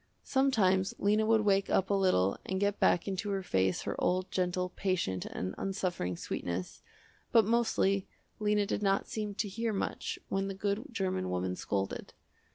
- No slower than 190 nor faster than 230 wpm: No, average, 165 wpm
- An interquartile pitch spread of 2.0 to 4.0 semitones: Yes, narrow, 2.6 semitones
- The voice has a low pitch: No, high, 195 Hz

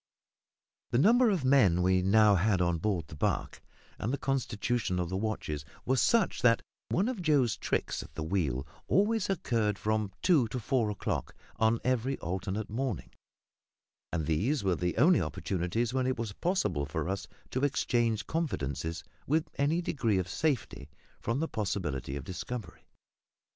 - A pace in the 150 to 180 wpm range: Yes, average, 160 wpm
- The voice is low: Yes, low, 110 Hz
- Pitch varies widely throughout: Yes, wide, 7.0 semitones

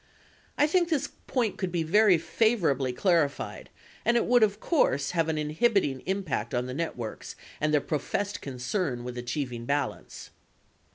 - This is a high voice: No, medium, 160 Hz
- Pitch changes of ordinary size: No, wide, 7.6 semitones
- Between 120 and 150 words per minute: No, average, 160 wpm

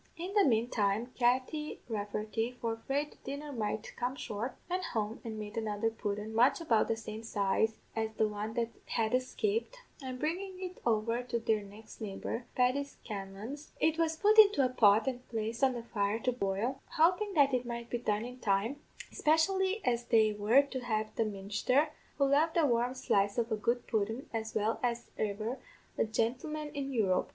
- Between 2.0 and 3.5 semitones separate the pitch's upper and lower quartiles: No, average, 4.2 semitones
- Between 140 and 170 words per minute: No, average, 185 wpm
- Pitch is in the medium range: No, high, 235 Hz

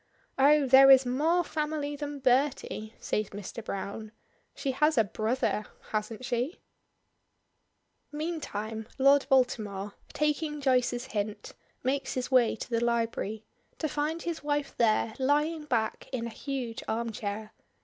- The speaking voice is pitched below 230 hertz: No, very high, 255 Hz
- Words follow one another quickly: No, slow, 135 wpm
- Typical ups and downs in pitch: Yes, average, 4.9 semitones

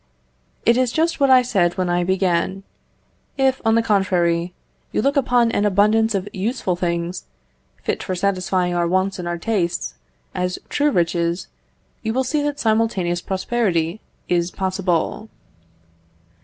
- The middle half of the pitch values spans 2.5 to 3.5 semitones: No, average, 4.5 semitones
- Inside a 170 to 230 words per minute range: No, average, 145 wpm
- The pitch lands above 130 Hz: Yes, high, 190 Hz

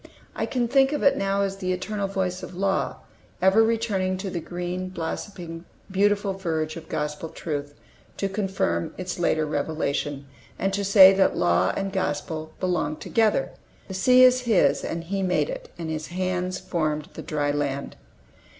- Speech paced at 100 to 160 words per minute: No, average, 170 wpm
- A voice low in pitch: No, medium, 185 Hz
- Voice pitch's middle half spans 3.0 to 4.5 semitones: Yes, average, 3.8 semitones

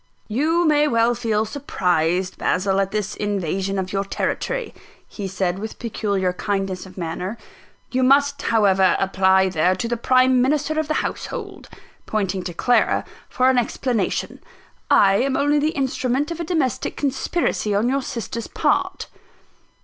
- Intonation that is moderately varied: No, wide, 6.2 semitones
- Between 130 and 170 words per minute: Yes, average, 150 wpm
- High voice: Yes, high, 225 Hz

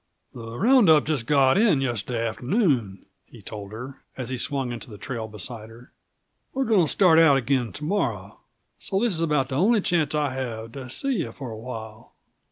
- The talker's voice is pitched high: No, low, 130 Hz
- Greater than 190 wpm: Yes, average, 200 wpm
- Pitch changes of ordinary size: No, wide, 5.8 semitones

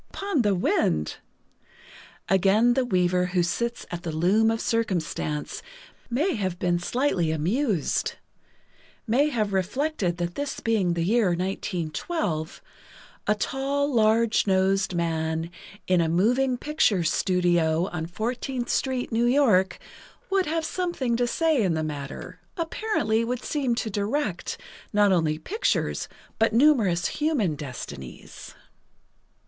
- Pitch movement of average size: No, wide, 6.4 semitones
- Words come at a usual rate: No, slow, 120 wpm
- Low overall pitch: No, high, 205 Hz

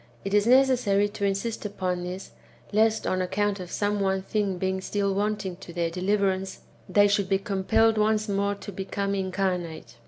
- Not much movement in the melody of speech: Yes, narrow, 1.6 semitones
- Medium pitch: No, high, 200 Hz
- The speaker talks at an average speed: Yes, average, 175 wpm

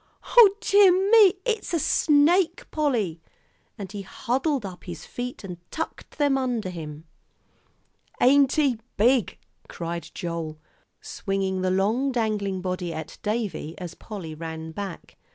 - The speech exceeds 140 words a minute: No, slow, 135 wpm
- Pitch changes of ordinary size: No, wide, 8.2 semitones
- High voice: Yes, high, 210 Hz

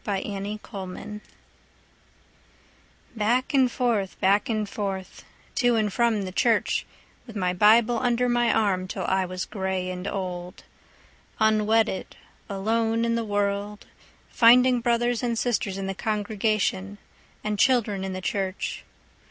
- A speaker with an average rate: No, slow, 130 wpm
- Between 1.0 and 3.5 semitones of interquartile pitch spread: Yes, average, 3.2 semitones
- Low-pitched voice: No, high, 210 Hz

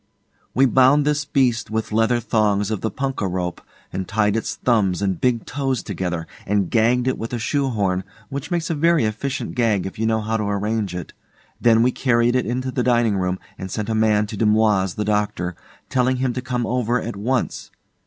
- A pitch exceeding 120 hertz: No, low, 110 Hz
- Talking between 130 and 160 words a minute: No, fast, 205 wpm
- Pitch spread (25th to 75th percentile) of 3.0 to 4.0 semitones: Yes, average, 3.6 semitones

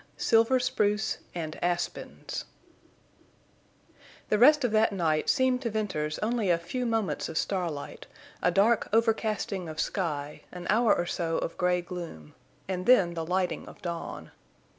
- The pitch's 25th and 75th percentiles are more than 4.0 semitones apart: Yes, average, 4.8 semitones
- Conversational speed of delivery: Yes, average, 145 wpm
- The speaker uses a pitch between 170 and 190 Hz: Yes, medium, 185 Hz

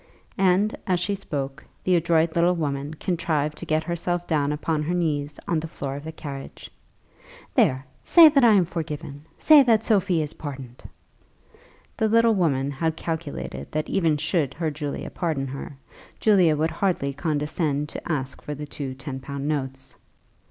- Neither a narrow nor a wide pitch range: Yes, average, 3.6 semitones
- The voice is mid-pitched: Yes, medium, 155 Hz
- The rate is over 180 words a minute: No, average, 165 wpm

